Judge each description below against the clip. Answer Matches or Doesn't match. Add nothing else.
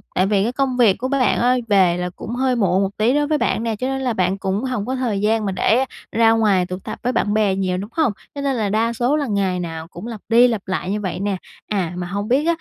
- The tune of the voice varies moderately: Matches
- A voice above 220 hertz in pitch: Doesn't match